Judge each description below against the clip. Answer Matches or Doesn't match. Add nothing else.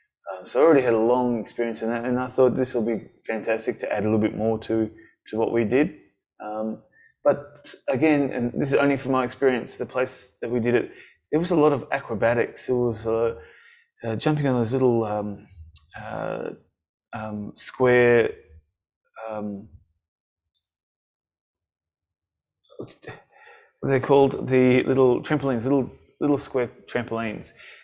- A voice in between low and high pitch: Doesn't match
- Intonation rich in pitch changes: Doesn't match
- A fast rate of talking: Doesn't match